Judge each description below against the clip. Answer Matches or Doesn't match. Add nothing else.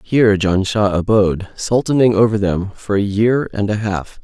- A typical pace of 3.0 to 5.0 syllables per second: Matches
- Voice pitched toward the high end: Doesn't match